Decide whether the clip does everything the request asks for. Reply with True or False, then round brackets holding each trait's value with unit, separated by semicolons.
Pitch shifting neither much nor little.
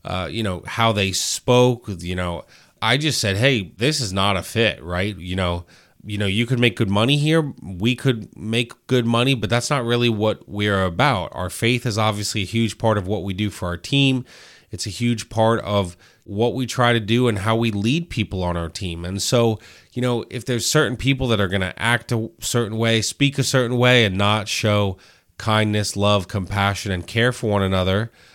True (3.4 semitones)